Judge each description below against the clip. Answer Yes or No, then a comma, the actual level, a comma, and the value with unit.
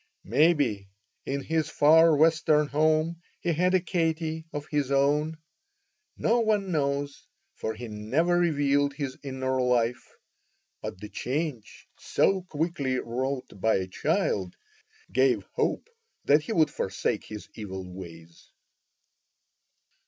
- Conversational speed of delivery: No, slow, 125 wpm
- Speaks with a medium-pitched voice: Yes, medium, 145 Hz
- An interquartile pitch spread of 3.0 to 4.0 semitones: No, average, 5.1 semitones